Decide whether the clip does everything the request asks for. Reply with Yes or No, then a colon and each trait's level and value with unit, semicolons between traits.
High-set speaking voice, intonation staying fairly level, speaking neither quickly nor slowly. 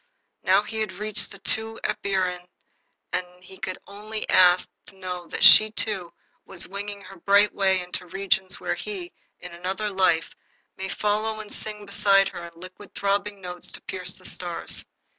Yes: high, 195 Hz; narrow, 2.3 semitones; average, 170 wpm